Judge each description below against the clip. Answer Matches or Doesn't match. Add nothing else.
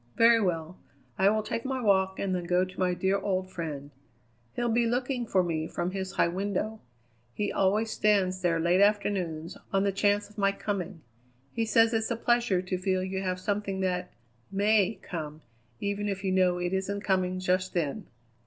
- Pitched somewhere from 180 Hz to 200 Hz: Matches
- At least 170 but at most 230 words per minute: Matches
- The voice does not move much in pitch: Matches